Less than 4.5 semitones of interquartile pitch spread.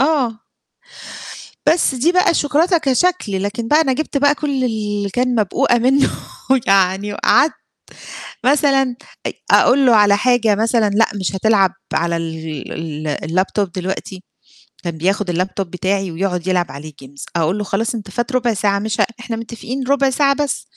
No: wide, 5.6 semitones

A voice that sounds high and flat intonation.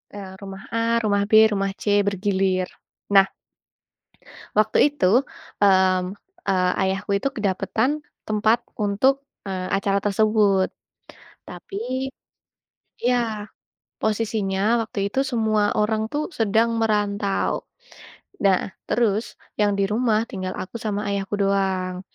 Yes: high, 205 Hz; narrow, 2.2 semitones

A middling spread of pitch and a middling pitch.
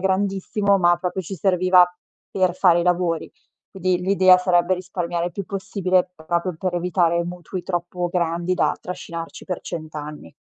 No: narrow, 1.4 semitones; medium, 180 Hz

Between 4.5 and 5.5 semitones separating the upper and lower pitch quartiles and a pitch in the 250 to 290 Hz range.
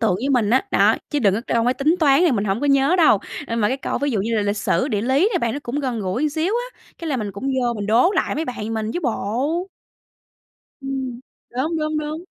Yes: average, 5.2 semitones; very high, 260 Hz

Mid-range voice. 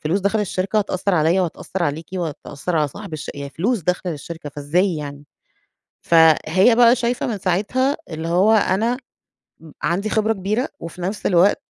Yes: medium, 180 Hz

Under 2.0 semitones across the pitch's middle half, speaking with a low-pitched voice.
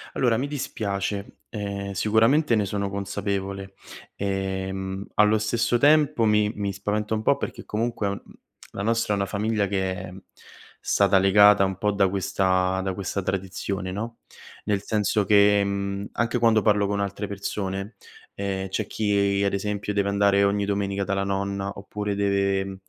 Yes: narrow, 1.3 semitones; low, 100 Hz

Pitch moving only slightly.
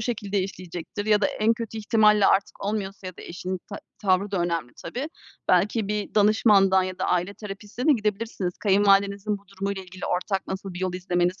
Yes: narrow, 2.1 semitones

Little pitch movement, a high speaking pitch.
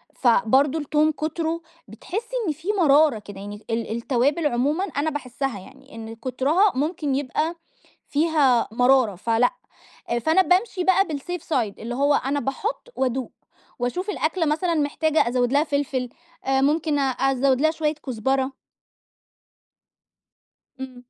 No: average, 4.1 semitones; very high, 280 Hz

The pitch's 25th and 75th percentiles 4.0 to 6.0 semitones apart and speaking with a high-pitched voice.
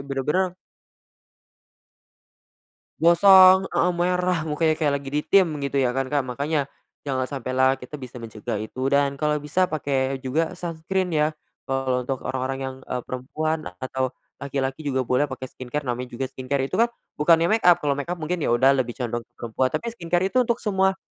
No: average, 4.5 semitones; medium, 140 Hz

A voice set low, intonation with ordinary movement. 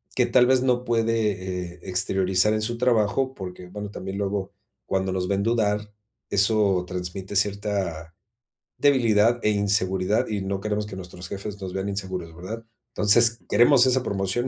Yes: low, 100 Hz; average, 3.0 semitones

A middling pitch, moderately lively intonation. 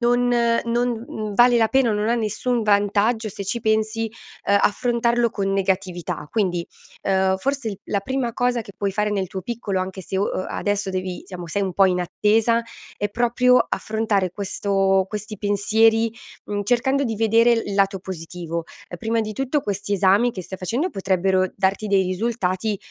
No: high, 205 Hz; average, 3.3 semitones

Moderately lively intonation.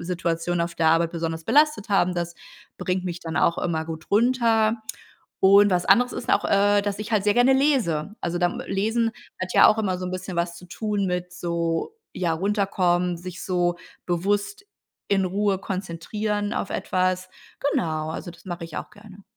Yes: average, 3.1 semitones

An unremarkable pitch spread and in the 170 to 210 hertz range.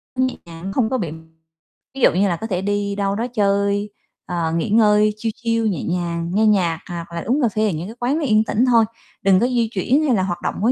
Yes: average, 4.2 semitones; high, 205 Hz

